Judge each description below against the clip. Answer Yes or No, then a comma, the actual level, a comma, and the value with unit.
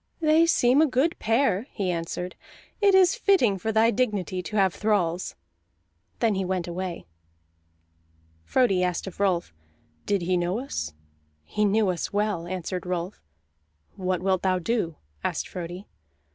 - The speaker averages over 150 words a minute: No, average, 145 wpm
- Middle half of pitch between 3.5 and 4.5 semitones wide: Yes, average, 4.0 semitones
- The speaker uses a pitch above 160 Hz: Yes, high, 190 Hz